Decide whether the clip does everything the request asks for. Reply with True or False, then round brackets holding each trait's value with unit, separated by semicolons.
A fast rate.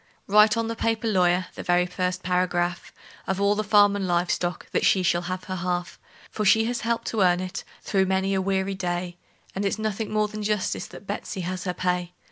True (220 wpm)